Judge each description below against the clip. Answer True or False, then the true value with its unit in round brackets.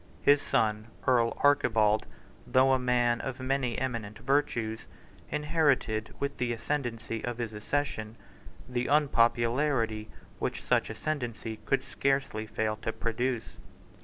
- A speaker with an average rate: False (120 wpm)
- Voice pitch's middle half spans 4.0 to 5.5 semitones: False (3.5 semitones)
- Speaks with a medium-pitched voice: False (120 Hz)